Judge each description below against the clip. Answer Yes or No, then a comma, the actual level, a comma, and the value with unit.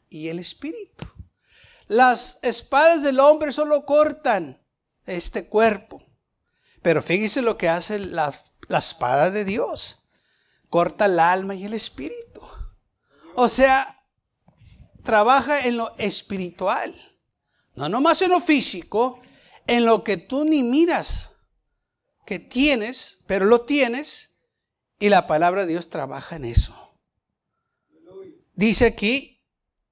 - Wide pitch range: Yes, wide, 6.4 semitones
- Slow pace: Yes, slow, 120 wpm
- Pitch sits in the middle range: No, high, 235 Hz